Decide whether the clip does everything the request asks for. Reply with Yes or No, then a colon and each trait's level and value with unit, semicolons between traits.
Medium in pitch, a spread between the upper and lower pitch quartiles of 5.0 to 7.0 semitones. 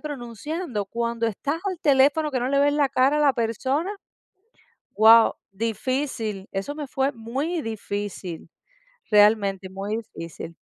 No: high, 235 Hz; wide, 5.5 semitones